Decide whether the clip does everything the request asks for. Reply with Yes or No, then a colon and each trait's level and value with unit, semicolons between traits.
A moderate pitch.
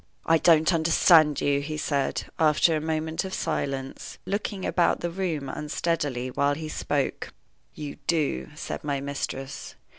Yes: medium, 155 Hz